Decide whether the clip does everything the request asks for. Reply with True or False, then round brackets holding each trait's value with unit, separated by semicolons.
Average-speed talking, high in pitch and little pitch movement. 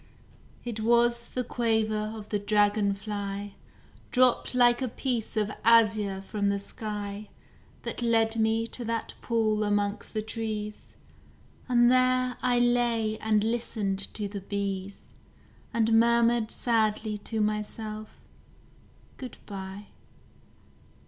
False (120 wpm; 220 Hz; 2.2 semitones)